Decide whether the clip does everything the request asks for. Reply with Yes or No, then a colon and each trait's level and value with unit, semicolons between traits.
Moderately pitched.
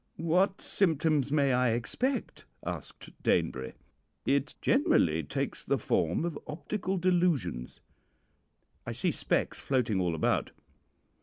Yes: medium, 145 Hz